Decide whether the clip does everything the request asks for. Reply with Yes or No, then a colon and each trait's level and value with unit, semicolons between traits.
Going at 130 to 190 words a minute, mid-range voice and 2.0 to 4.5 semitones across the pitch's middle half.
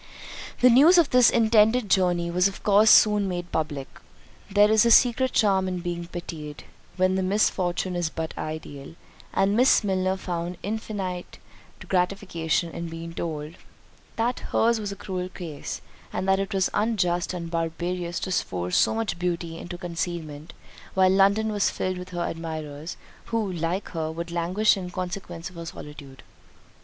Yes: average, 160 wpm; medium, 180 Hz; average, 3.2 semitones